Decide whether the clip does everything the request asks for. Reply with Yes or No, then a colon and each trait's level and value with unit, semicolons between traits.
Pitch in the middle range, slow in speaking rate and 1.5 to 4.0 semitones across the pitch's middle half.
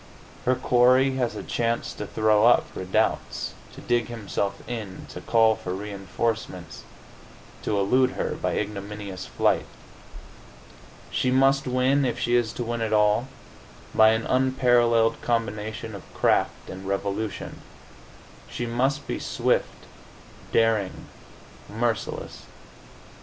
No: low, 115 Hz; slow, 120 wpm; average, 2.8 semitones